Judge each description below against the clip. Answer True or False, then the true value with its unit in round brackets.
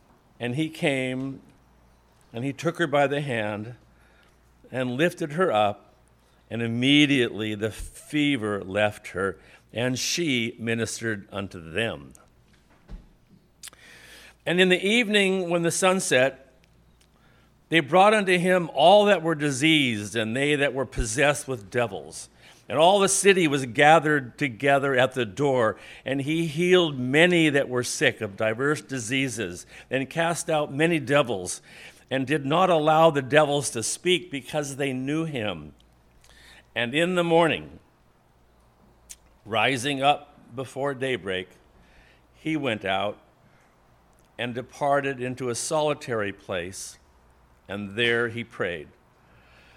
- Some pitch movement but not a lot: False (6.0 semitones)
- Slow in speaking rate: True (130 wpm)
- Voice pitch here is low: True (130 Hz)